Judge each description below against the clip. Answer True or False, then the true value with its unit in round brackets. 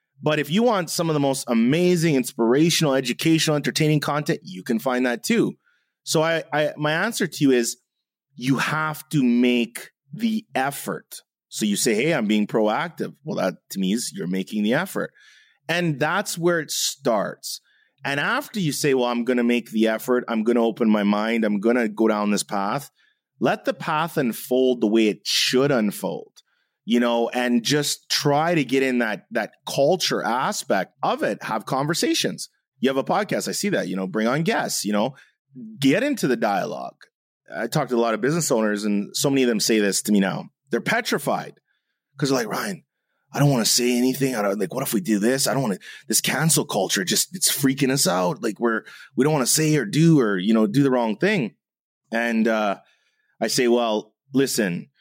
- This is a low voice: True (130 Hz)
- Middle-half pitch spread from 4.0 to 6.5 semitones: True (5.2 semitones)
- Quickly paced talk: True (210 wpm)